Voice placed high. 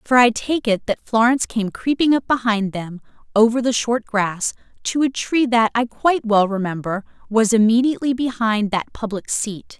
Yes: high, 225 Hz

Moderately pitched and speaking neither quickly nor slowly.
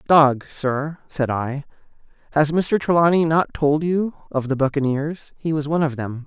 Yes: medium, 150 Hz; average, 170 wpm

